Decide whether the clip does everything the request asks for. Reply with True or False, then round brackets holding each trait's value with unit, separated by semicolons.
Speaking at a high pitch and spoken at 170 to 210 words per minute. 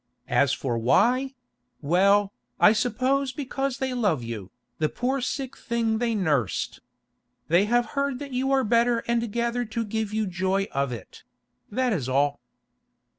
False (220 Hz; 150 wpm)